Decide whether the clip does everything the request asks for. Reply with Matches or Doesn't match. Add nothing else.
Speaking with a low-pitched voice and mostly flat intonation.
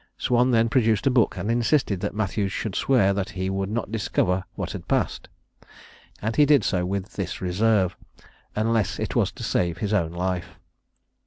Doesn't match